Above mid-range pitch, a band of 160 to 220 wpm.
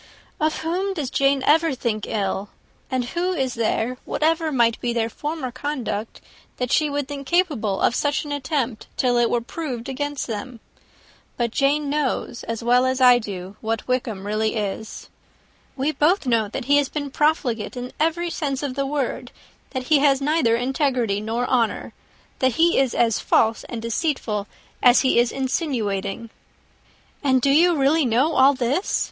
Yes: very high, 260 Hz; average, 170 wpm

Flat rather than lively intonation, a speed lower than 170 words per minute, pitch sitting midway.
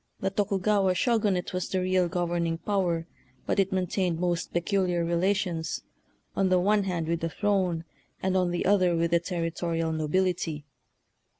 Yes: narrow, 2.2 semitones; average, 155 wpm; medium, 180 Hz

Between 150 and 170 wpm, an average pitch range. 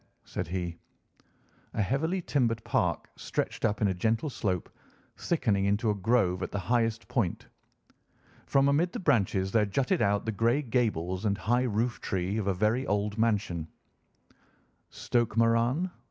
Yes: average, 155 wpm; average, 3.7 semitones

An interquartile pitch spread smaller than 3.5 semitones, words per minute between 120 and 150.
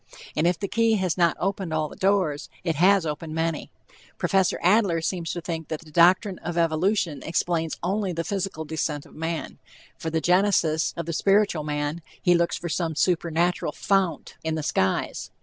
No: average, 2.8 semitones; average, 185 wpm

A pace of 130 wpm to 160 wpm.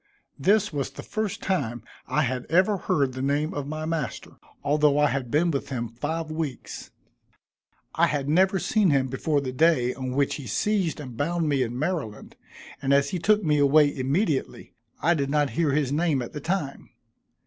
No: average, 190 wpm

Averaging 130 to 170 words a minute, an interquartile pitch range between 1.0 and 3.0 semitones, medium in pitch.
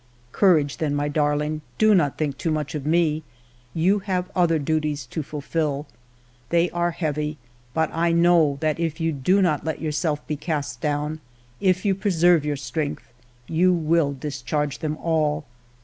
Yes: average, 165 wpm; narrow, 2.5 semitones; medium, 155 Hz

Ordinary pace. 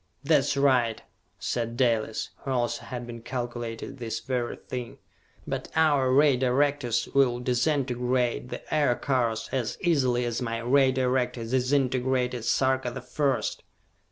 No: slow, 130 wpm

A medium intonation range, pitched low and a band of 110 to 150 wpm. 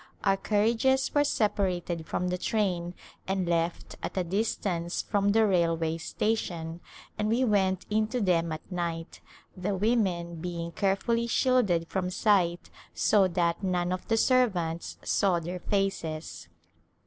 No: average, 3.7 semitones; medium, 185 Hz; slow, 135 wpm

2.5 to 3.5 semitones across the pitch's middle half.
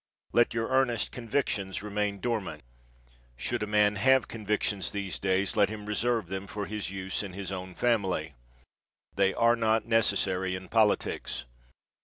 Yes: average, 2.9 semitones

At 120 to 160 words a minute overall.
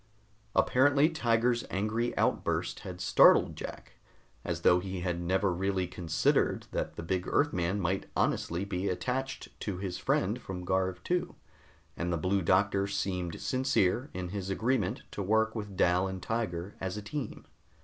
Yes: average, 155 wpm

